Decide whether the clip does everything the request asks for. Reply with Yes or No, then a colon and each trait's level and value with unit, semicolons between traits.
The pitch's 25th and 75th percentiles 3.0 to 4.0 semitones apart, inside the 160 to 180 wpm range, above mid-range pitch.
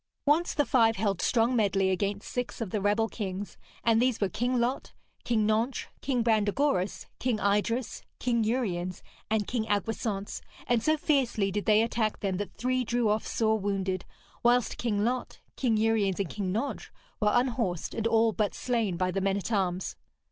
Yes: average, 3.3 semitones; average, 175 wpm; high, 220 Hz